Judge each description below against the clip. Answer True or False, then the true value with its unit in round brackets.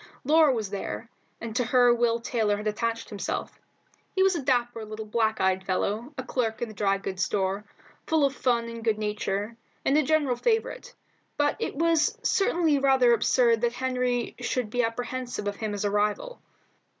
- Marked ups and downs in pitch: False (3.9 semitones)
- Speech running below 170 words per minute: False (185 wpm)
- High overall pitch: True (235 Hz)